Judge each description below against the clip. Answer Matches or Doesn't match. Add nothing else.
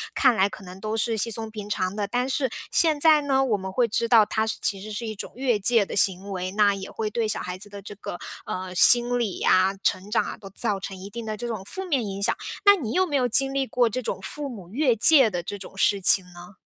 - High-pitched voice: Matches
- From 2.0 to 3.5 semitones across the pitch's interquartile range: Doesn't match